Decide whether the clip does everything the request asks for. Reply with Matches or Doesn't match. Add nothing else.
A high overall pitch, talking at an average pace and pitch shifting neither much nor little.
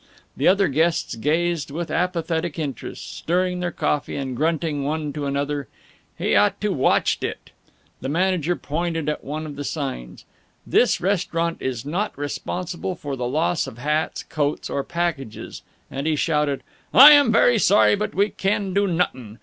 Doesn't match